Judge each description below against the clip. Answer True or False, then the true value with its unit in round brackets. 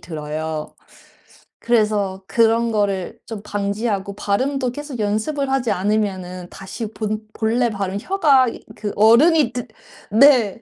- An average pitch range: True (3.7 semitones)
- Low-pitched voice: False (215 Hz)